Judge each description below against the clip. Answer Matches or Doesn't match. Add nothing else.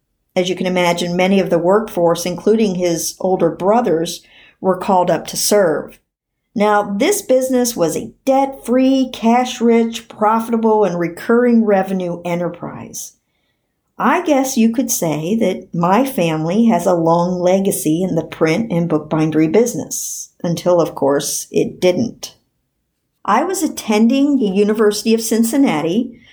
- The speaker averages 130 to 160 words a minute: Matches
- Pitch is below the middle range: Doesn't match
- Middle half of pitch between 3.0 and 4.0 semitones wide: Doesn't match